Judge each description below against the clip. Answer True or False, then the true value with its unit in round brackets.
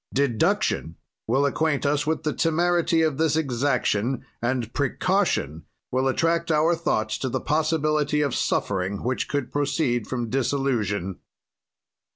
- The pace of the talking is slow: True (130 wpm)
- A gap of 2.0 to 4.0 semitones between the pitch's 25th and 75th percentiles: False (4.7 semitones)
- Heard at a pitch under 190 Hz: True (140 Hz)